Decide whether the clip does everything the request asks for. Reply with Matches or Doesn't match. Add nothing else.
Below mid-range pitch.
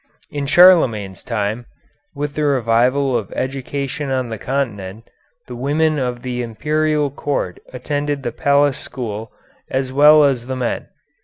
Matches